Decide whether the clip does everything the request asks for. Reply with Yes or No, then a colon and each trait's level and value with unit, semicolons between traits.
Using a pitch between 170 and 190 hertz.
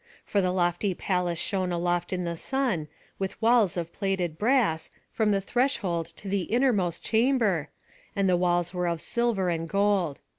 Yes: medium, 185 Hz